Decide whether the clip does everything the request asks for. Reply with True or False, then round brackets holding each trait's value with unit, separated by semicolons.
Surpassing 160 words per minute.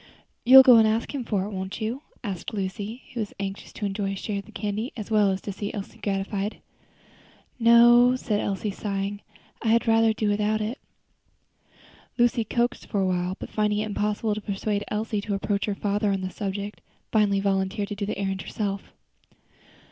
True (195 wpm)